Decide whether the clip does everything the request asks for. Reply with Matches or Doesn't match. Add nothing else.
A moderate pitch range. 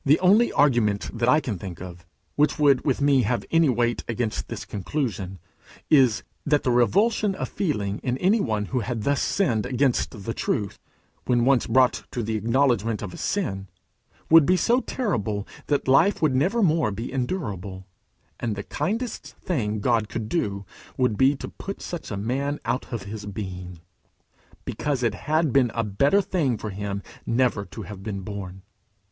Doesn't match